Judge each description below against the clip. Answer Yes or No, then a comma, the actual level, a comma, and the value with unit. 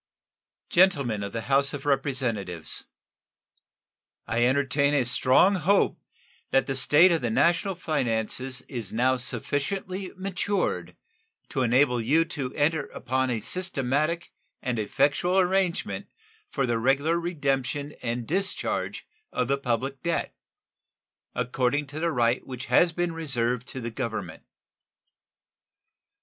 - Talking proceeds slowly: Yes, slow, 125 wpm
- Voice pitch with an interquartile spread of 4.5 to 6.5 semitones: Yes, average, 5.0 semitones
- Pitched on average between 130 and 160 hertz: Yes, low, 135 Hz